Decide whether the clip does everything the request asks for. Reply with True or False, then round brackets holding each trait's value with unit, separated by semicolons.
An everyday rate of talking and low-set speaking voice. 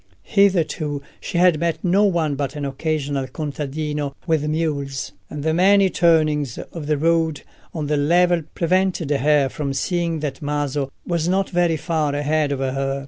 False (160 wpm; 155 Hz)